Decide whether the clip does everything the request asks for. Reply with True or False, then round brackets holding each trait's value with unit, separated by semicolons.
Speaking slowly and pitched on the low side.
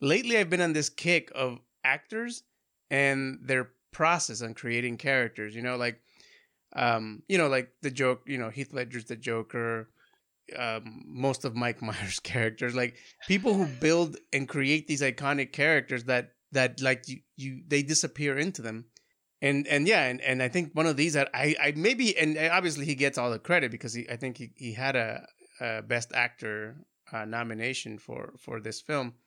False (185 wpm; 130 Hz)